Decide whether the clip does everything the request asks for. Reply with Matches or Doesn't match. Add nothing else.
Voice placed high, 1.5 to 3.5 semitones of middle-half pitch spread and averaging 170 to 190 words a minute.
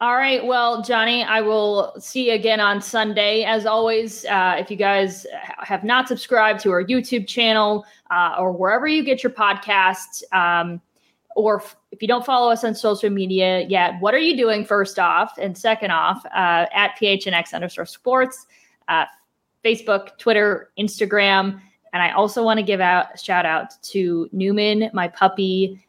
Matches